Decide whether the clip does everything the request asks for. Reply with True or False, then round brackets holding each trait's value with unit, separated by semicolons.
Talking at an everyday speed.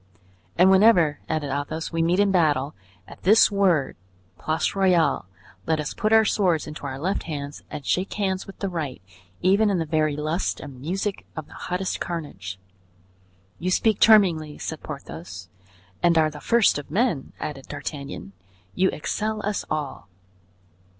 True (160 wpm)